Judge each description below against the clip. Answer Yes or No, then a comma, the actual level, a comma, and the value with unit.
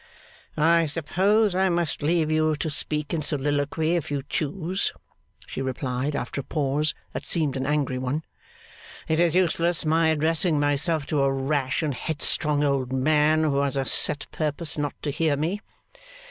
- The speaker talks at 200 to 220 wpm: No, average, 165 wpm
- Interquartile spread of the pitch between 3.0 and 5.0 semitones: No, narrow, 2.5 semitones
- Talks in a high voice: No, medium, 150 Hz